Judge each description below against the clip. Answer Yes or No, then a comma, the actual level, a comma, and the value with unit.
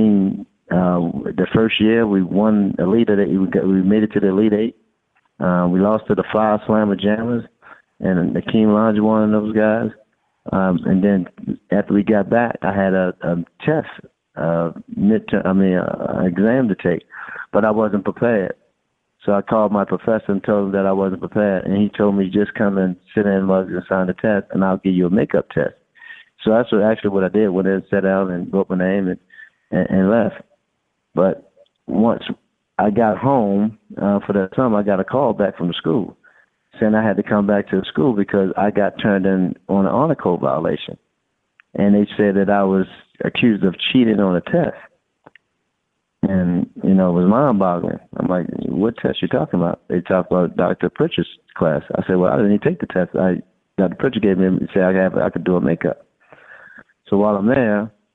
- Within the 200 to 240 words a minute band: Yes, fast, 205 wpm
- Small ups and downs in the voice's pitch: Yes, narrow, 2.2 semitones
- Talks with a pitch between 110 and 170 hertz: No, low, 100 Hz